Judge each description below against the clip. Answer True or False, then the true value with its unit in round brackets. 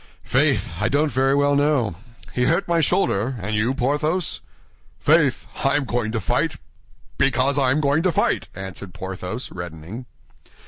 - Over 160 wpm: False (150 wpm)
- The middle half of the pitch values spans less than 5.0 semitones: False (5.6 semitones)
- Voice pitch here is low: True (130 Hz)